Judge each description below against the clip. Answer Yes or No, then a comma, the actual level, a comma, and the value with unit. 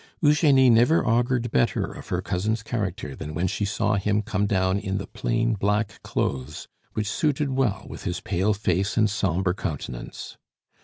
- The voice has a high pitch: No, low, 105 Hz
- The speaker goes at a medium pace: Yes, average, 165 wpm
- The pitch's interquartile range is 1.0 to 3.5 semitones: No, average, 3.9 semitones